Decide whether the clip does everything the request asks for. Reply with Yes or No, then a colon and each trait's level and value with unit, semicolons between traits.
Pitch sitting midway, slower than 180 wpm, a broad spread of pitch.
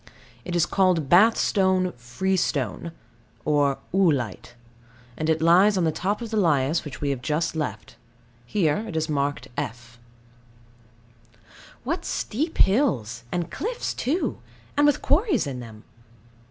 Yes: medium, 160 Hz; average, 140 wpm; wide, 6.2 semitones